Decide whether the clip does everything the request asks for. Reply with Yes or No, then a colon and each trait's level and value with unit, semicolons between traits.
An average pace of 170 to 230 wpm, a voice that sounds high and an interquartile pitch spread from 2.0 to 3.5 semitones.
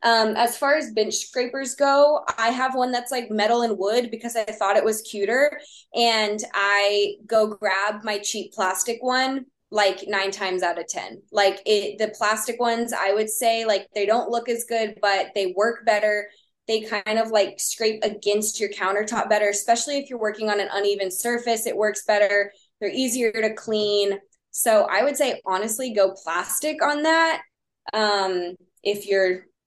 Yes: average, 180 wpm; high, 215 Hz; narrow, 2.6 semitones